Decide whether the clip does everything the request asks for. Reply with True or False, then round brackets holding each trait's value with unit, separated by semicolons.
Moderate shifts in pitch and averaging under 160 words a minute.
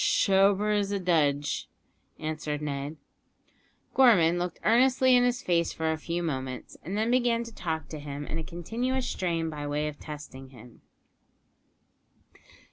False (6.1 semitones; 150 wpm)